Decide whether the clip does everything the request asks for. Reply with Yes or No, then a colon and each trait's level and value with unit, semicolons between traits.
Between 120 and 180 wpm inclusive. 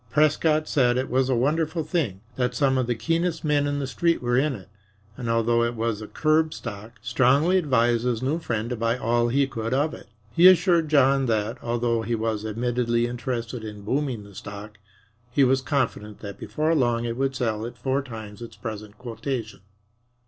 No: average, 195 wpm